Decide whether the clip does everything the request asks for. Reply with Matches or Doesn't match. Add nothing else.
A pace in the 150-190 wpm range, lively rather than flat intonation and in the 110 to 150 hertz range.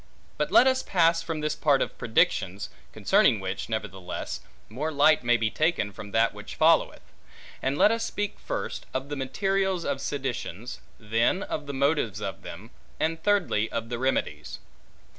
Matches